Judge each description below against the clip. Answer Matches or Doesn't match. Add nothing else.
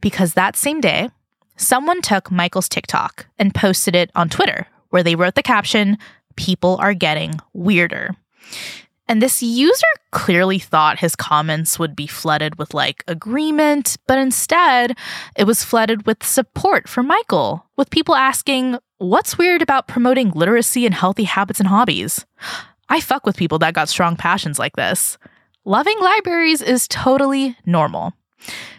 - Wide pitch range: Matches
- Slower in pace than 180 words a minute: Matches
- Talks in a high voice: Matches